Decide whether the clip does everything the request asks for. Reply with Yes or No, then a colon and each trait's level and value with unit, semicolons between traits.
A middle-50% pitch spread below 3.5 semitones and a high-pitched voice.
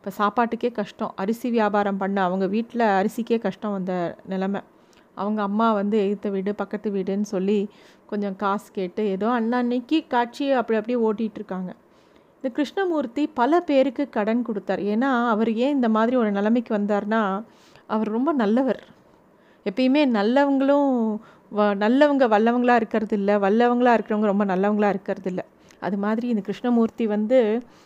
Yes: average, 3.1 semitones; high, 220 Hz